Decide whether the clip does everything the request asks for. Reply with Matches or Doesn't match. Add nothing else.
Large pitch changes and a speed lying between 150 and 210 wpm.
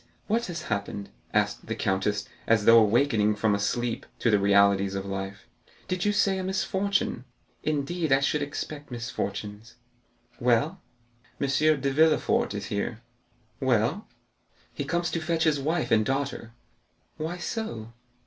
Doesn't match